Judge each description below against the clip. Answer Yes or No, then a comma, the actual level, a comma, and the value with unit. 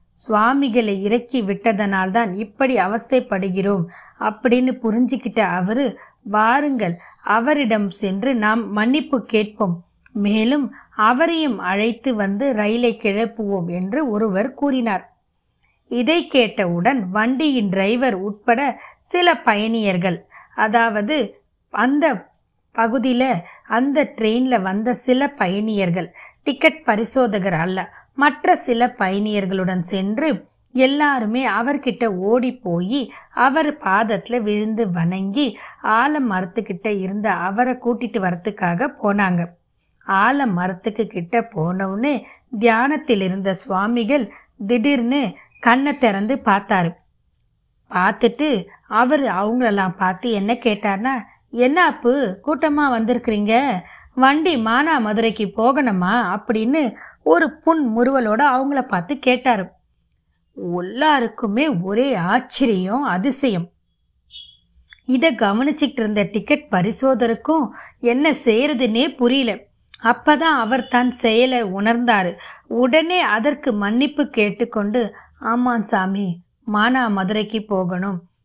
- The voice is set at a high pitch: Yes, high, 230 Hz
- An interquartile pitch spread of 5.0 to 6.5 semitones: No, average, 4.5 semitones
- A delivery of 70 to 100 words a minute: Yes, average, 90 wpm